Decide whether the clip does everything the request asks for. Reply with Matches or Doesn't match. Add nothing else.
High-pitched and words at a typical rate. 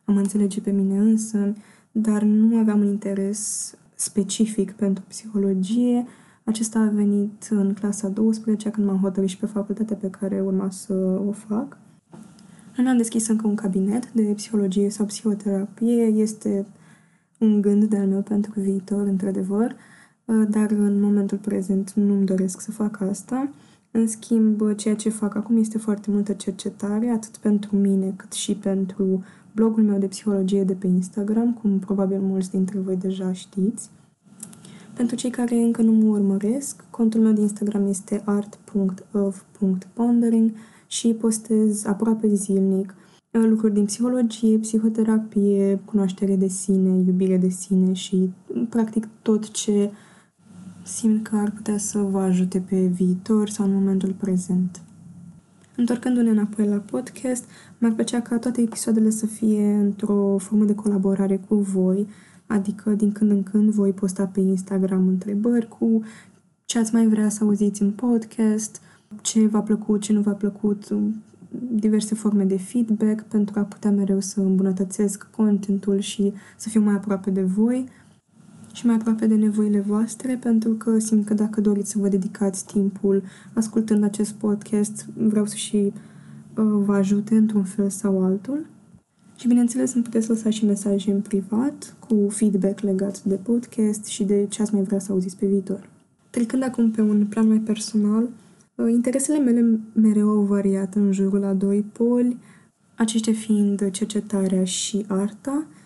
Matches